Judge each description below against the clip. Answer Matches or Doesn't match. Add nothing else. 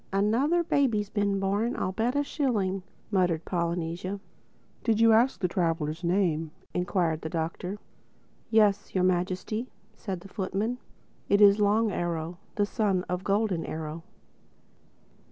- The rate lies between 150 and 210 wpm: Doesn't match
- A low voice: Doesn't match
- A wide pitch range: Doesn't match